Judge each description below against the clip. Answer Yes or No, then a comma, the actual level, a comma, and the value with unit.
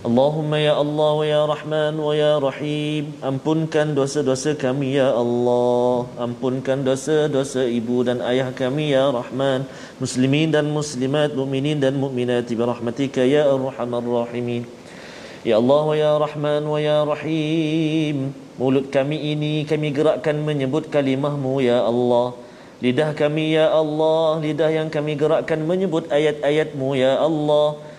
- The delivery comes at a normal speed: No, fast, 135 wpm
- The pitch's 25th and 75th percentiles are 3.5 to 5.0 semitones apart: No, narrow, 2.6 semitones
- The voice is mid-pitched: Yes, medium, 145 Hz